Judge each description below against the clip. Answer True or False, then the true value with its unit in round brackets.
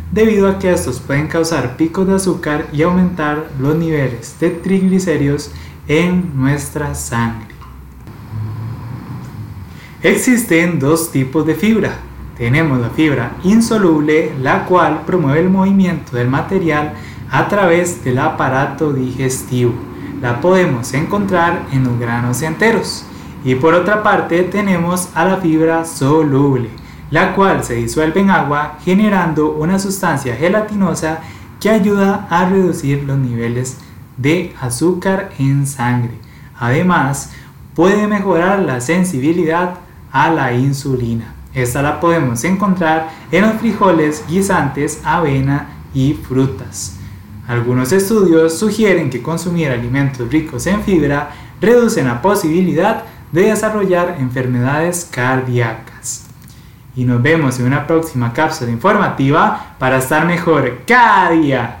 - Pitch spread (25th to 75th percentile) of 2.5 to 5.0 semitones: False (5.6 semitones)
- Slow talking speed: True (120 wpm)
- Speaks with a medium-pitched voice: True (155 Hz)